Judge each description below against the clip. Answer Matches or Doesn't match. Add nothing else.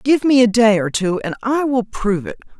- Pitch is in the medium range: Doesn't match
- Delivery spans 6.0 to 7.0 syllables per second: Doesn't match